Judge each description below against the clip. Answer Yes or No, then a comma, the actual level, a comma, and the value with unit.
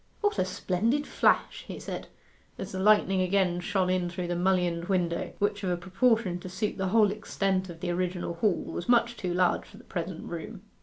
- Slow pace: No, fast, 205 wpm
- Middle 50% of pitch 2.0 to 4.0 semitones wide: Yes, narrow, 2.5 semitones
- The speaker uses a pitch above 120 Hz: Yes, medium, 185 Hz